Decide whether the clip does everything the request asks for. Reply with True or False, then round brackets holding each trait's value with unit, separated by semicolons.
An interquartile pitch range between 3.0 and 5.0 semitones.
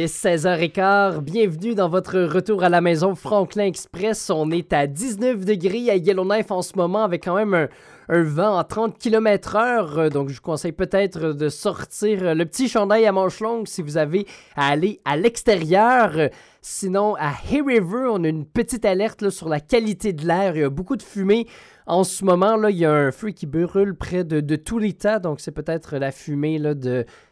True (4.5 semitones)